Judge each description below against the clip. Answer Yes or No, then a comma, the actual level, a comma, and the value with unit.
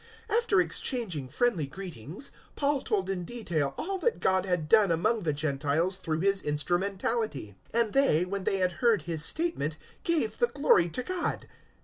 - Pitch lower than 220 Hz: Yes, high, 190 Hz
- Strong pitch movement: Yes, wide, 7.3 semitones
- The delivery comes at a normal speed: Yes, average, 170 wpm